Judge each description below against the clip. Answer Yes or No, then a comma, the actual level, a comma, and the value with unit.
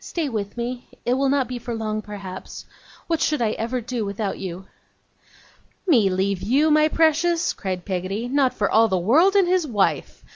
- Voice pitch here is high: Yes, high, 235 Hz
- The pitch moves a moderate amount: No, wide, 6.7 semitones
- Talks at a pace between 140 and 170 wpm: No, average, 185 wpm